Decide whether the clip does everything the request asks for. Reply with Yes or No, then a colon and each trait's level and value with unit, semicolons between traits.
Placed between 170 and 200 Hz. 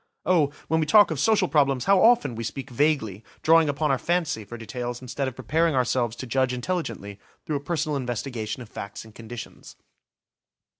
No: low, 135 Hz